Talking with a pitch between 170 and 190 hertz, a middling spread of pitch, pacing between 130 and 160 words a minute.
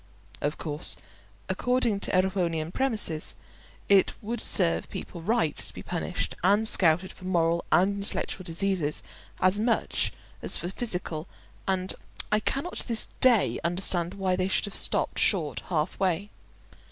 Yes: medium, 185 Hz; average, 3.4 semitones; average, 145 wpm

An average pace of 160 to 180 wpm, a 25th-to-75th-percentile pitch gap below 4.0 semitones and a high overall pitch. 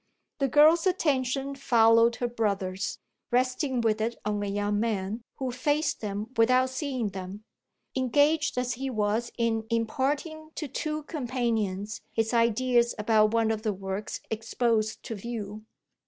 No: average, 140 wpm; average, 3.4 semitones; high, 230 Hz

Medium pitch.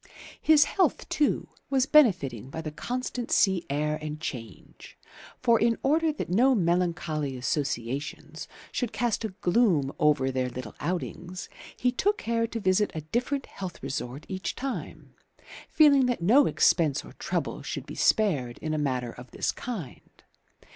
Yes: medium, 180 Hz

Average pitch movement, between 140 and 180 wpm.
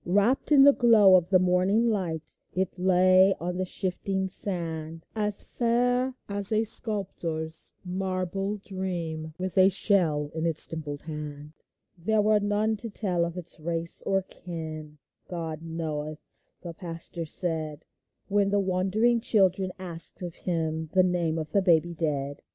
Yes: average, 3.6 semitones; average, 150 wpm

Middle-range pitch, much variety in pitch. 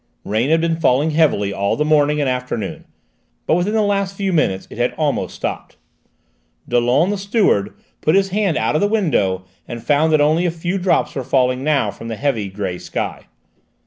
Yes: medium, 150 Hz; wide, 6.7 semitones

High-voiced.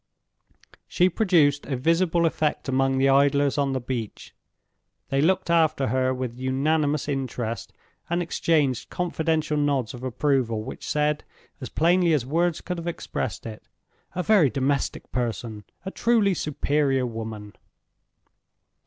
No: medium, 145 Hz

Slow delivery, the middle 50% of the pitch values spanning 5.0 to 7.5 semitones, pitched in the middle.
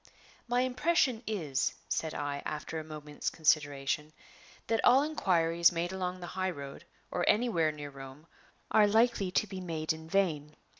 No: average, 155 wpm; wide, 5.4 semitones; medium, 170 Hz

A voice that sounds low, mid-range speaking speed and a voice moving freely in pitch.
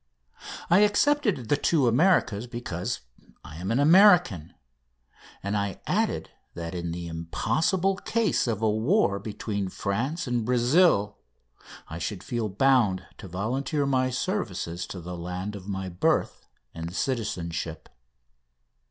No: low, 110 Hz; slow, 130 wpm; wide, 7.6 semitones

